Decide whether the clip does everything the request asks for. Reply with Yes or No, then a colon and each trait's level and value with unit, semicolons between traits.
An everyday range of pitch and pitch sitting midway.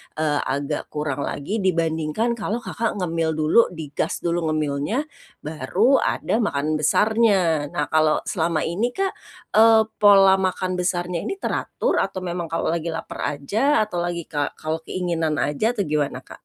Yes: average, 5.0 semitones; medium, 170 Hz